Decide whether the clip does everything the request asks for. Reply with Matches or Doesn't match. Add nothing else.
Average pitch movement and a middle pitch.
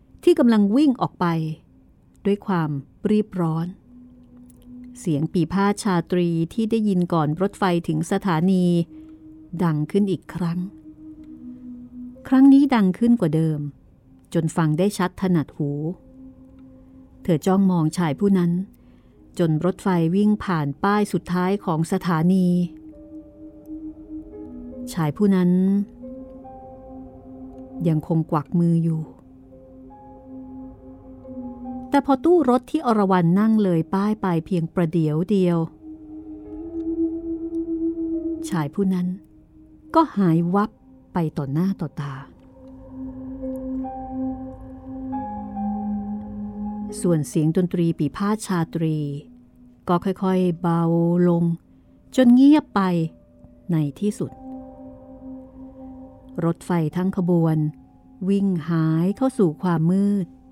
Doesn't match